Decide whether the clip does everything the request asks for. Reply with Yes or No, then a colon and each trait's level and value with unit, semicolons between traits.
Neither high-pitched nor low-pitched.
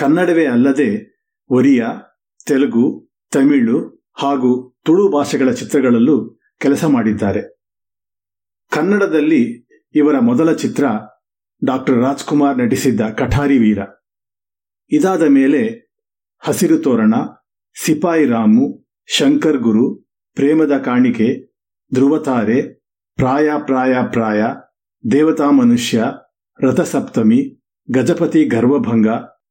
Yes: medium, 145 Hz